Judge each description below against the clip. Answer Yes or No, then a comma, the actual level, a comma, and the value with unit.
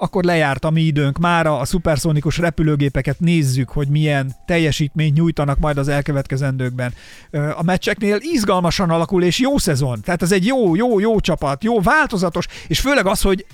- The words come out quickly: Yes, fast, 165 wpm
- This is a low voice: No, medium, 165 Hz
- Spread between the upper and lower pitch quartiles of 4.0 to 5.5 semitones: Yes, average, 4.5 semitones